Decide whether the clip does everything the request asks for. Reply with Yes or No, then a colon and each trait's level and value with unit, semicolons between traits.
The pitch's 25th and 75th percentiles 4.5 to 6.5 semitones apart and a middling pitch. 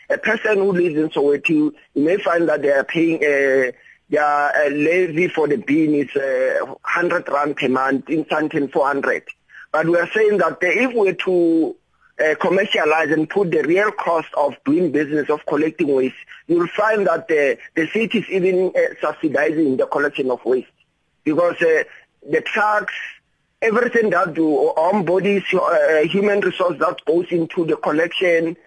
Yes: average, 4.9 semitones; medium, 175 Hz